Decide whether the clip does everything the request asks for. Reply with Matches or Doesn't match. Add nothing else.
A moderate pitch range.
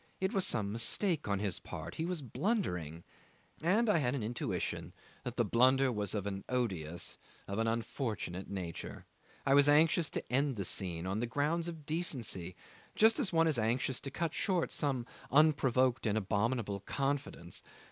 Doesn't match